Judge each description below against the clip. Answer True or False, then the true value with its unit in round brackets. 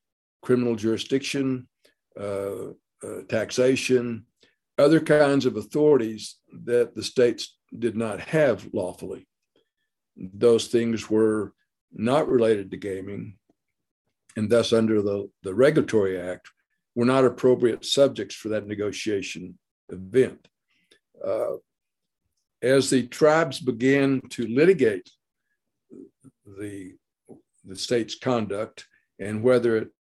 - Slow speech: True (105 wpm)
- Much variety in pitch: False (3.8 semitones)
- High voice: False (120 Hz)